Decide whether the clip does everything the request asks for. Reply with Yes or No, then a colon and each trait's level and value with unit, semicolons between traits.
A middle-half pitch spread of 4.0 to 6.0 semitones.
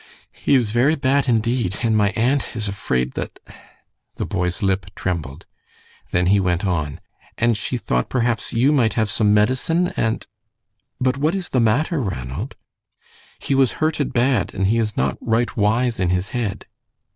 Yes: average, 5.1 semitones